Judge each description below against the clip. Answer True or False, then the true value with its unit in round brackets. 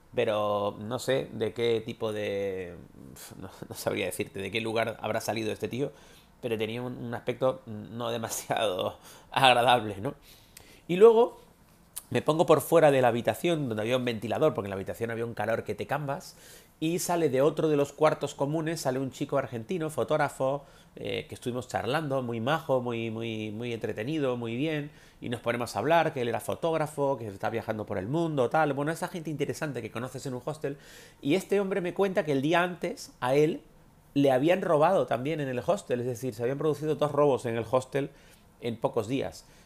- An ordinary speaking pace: False (195 wpm)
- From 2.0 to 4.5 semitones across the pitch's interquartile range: False (5.1 semitones)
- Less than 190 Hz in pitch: True (135 Hz)